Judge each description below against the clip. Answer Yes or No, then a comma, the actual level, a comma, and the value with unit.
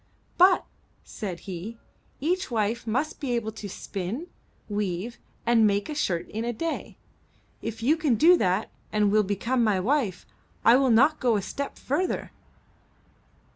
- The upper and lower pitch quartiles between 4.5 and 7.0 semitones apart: Yes, average, 5.1 semitones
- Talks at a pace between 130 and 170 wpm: Yes, average, 155 wpm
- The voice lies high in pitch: Yes, high, 230 Hz